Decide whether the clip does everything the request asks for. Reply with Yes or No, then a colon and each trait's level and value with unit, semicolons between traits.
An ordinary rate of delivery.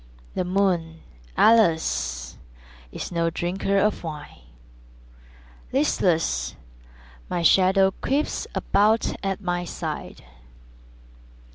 No: slow, 85 wpm